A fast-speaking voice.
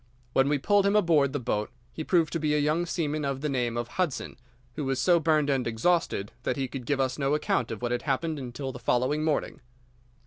Yes: fast, 235 wpm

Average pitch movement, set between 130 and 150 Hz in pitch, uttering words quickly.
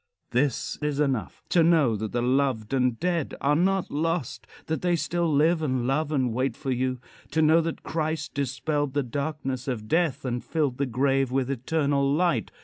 No: average, 3.7 semitones; medium, 140 Hz; average, 185 wpm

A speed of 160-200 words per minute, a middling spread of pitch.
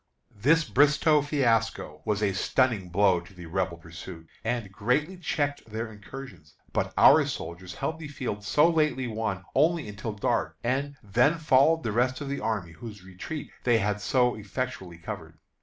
No: average, 165 wpm; wide, 6.5 semitones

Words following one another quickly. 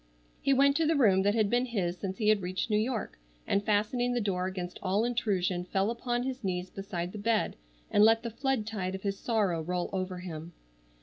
Yes: fast, 220 wpm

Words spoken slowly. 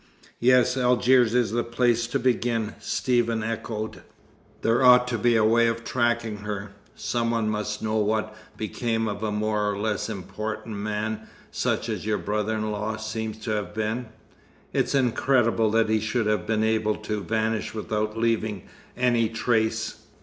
No: average, 165 wpm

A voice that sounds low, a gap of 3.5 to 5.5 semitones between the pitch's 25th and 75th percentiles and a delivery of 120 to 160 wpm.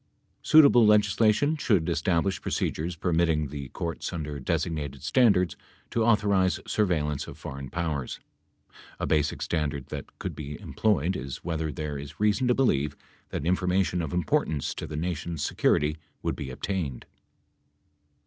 Yes: very low, 80 Hz; average, 4.6 semitones; average, 140 wpm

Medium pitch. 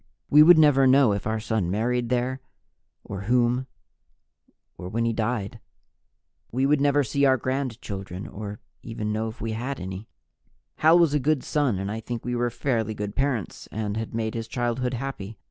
No: low, 120 Hz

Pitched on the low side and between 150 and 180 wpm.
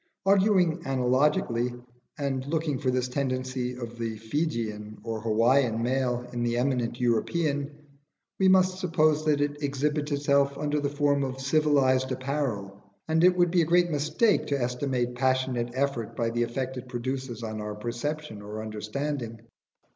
Yes: low, 130 Hz; average, 155 wpm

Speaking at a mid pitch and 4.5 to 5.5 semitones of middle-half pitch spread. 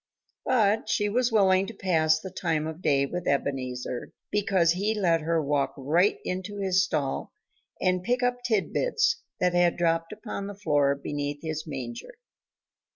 Yes: medium, 175 Hz; average, 5.1 semitones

